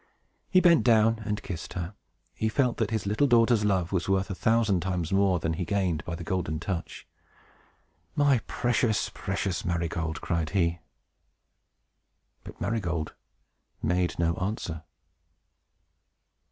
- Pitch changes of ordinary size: Yes, average, 4.5 semitones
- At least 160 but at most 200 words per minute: No, average, 140 wpm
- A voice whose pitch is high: No, very low, 95 Hz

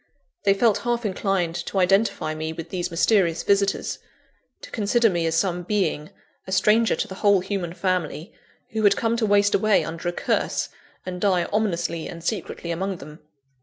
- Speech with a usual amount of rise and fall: Yes, average, 3.4 semitones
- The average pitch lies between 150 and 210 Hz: Yes, high, 190 Hz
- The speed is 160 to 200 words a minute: Yes, average, 175 wpm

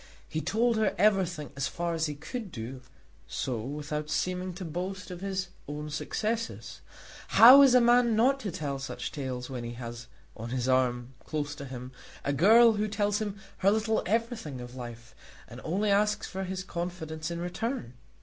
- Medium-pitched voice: Yes, medium, 175 Hz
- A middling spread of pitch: No, wide, 7.7 semitones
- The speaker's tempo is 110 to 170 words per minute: No, average, 180 wpm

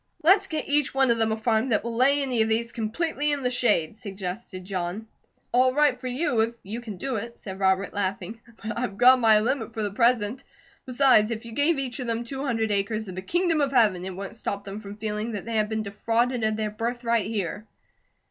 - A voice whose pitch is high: Yes, high, 225 Hz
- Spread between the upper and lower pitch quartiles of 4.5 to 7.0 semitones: No, average, 3.4 semitones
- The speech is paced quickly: Yes, fast, 230 wpm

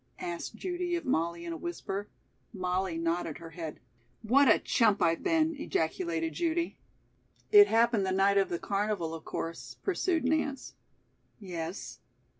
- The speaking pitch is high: Yes, high, 195 Hz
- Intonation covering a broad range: Yes, wide, 8.6 semitones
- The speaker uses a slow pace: No, average, 145 wpm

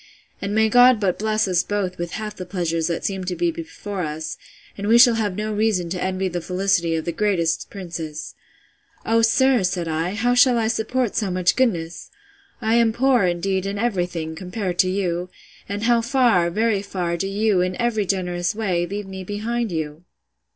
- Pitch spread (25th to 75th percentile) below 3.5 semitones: No, average, 4.0 semitones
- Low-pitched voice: No, high, 195 Hz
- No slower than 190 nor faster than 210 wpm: Yes, average, 195 wpm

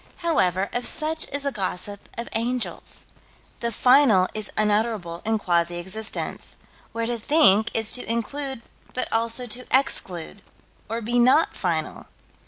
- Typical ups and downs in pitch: Yes, average, 4.1 semitones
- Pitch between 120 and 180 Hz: No, high, 225 Hz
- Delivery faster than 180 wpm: No, average, 140 wpm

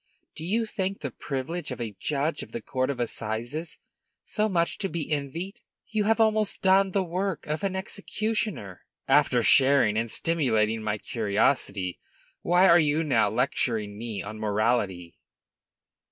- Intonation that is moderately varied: No, wide, 9.0 semitones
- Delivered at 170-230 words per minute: No, average, 155 wpm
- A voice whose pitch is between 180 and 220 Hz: No, medium, 140 Hz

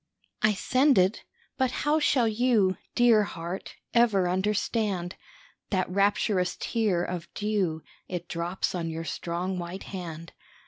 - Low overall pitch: No, high, 190 Hz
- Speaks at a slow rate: Yes, slow, 130 wpm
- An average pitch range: Yes, average, 3.7 semitones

